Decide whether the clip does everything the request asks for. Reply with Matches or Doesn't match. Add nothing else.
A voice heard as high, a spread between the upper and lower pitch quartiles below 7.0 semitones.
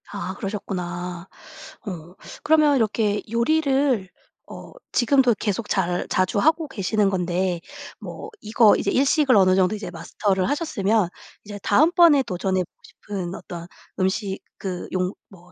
Matches